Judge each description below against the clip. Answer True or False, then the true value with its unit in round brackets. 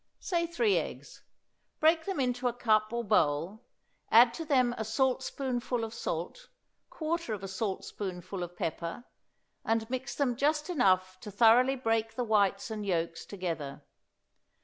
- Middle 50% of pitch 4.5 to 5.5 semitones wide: True (5.2 semitones)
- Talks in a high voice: True (225 Hz)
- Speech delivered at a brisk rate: False (150 wpm)